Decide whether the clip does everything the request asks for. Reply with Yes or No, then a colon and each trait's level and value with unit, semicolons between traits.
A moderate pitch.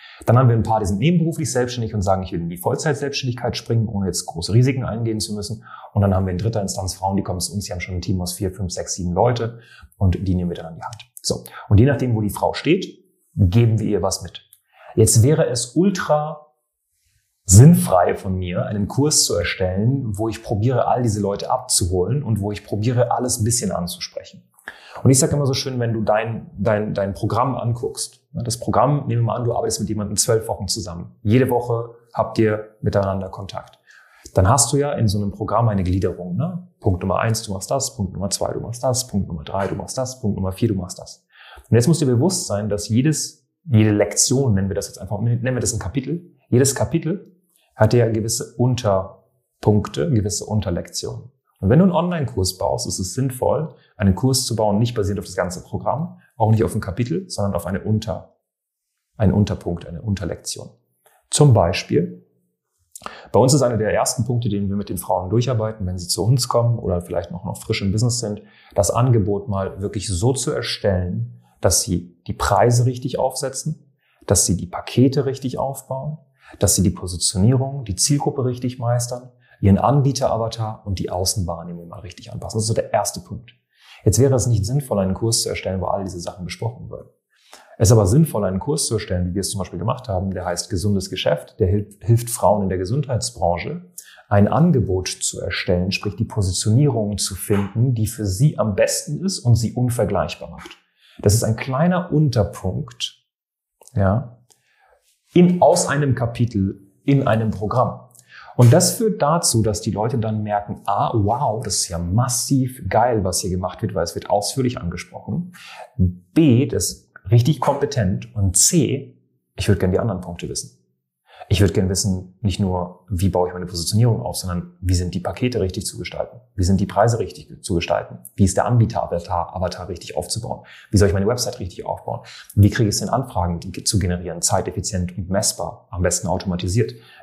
No: low, 110 Hz